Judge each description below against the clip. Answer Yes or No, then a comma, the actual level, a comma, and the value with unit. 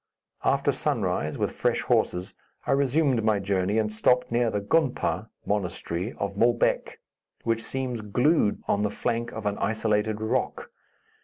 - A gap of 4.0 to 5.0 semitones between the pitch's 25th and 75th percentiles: No, average, 3.0 semitones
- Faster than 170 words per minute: No, average, 145 wpm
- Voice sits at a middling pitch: No, low, 110 Hz